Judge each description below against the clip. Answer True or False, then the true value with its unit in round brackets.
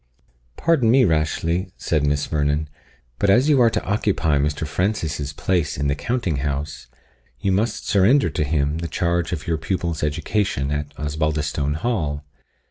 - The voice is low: True (80 Hz)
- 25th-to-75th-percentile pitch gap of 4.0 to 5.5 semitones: True (5.0 semitones)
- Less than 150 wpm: False (155 wpm)